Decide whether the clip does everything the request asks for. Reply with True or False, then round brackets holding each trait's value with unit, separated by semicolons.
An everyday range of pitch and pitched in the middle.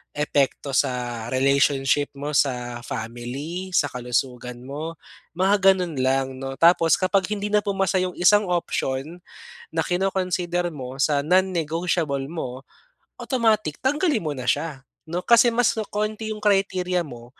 False (6.2 semitones; 165 Hz)